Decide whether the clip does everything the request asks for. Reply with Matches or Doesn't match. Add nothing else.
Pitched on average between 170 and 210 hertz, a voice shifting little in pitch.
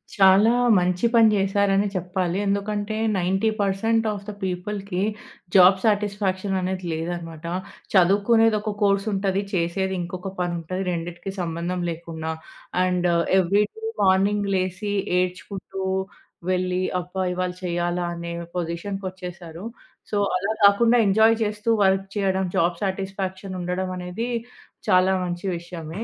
Matches